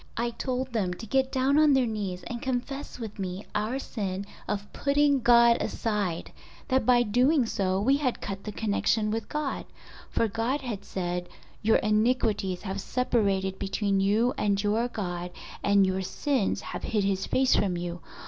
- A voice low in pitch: No, high, 215 Hz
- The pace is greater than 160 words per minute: Yes, average, 170 wpm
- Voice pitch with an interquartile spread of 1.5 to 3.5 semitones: No, average, 4.4 semitones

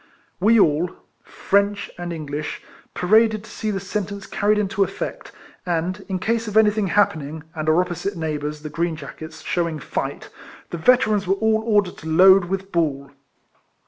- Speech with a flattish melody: No, average, 4.5 semitones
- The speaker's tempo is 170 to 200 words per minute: No, average, 160 wpm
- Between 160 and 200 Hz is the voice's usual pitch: Yes, medium, 185 Hz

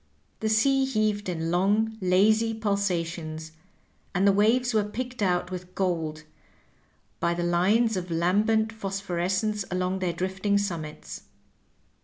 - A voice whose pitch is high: Yes, high, 195 Hz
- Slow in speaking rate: Yes, slow, 125 wpm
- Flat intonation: No, average, 3.6 semitones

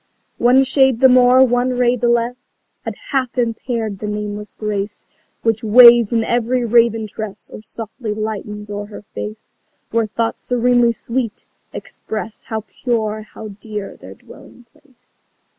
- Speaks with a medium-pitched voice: No, high, 230 Hz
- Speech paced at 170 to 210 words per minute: No, average, 145 wpm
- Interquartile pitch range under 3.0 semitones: Yes, narrow, 2.6 semitones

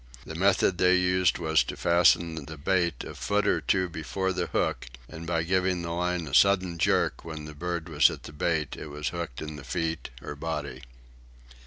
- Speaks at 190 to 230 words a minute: Yes, average, 200 wpm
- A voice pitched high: No, very low, 85 Hz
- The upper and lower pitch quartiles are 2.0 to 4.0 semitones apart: Yes, average, 2.7 semitones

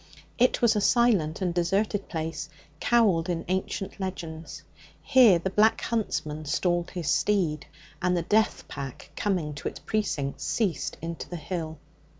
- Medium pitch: Yes, medium, 180 Hz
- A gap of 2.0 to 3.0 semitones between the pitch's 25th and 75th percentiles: No, average, 4.5 semitones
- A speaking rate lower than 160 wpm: Yes, average, 150 wpm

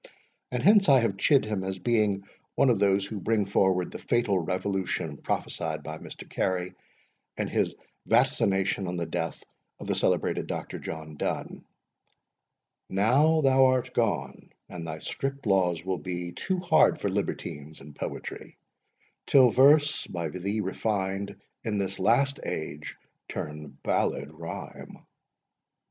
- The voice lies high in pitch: No, low, 100 Hz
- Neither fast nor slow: Yes, average, 145 wpm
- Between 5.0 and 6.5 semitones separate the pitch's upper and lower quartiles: Yes, wide, 5.5 semitones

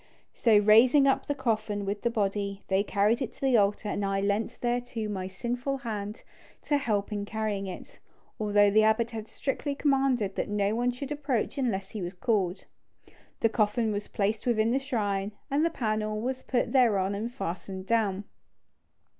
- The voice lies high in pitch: Yes, high, 215 Hz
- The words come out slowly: No, average, 180 wpm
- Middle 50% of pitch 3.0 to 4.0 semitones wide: Yes, average, 3.3 semitones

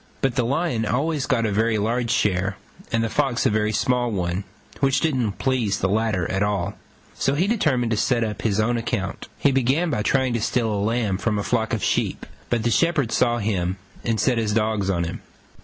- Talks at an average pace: No, fast, 220 wpm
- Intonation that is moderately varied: Yes, average, 3.5 semitones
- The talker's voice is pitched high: No, low, 115 Hz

